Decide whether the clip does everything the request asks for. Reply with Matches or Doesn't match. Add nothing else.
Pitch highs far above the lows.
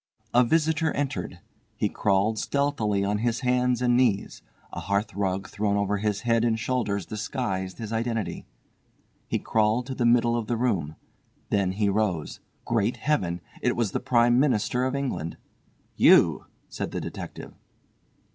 Doesn't match